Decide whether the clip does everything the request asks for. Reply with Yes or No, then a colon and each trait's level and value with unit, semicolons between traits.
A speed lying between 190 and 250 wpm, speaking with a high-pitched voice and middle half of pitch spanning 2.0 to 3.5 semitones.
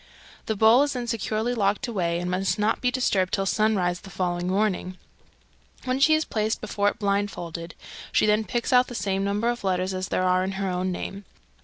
Yes: fast, 205 wpm; high, 200 Hz; average, 3.2 semitones